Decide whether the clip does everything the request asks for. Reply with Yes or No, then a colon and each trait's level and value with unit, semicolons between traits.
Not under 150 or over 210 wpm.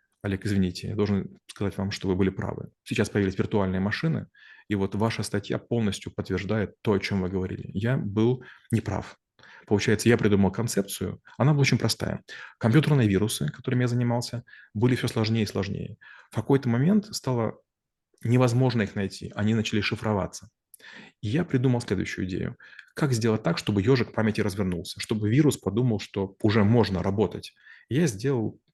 Yes: fast, 160 wpm